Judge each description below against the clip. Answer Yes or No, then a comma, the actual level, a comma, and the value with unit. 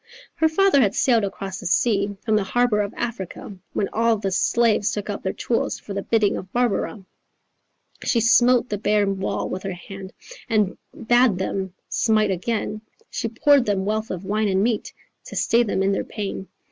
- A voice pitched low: No, high, 210 Hz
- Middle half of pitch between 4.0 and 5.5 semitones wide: No, average, 3.0 semitones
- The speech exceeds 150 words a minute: Yes, average, 185 wpm